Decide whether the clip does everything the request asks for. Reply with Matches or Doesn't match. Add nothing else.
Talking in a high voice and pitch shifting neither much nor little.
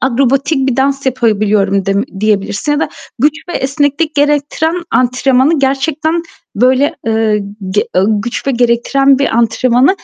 Matches